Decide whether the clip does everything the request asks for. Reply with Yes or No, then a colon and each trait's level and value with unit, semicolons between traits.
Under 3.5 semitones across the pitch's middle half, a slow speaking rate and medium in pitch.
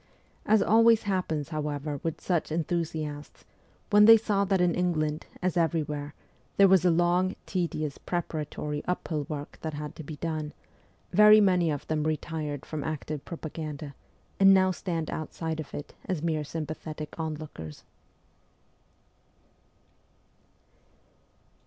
Yes: average, 3.1 semitones; slow, 130 wpm; medium, 160 Hz